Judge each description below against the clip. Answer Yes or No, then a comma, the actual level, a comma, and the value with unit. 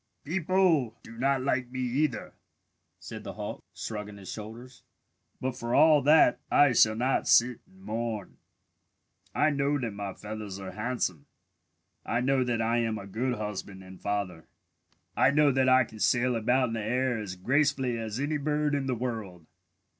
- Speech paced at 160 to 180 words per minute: Yes, average, 170 wpm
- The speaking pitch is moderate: No, low, 120 Hz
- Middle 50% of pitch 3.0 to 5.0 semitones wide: Yes, average, 4.1 semitones